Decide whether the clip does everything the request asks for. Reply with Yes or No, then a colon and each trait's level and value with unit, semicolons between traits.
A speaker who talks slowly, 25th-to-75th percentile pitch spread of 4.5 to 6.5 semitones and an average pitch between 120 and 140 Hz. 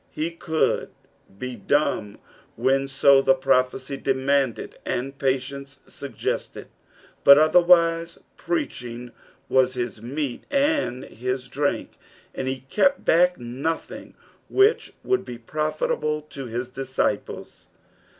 No: slow, 110 wpm; average, 3.6 semitones; low, 135 Hz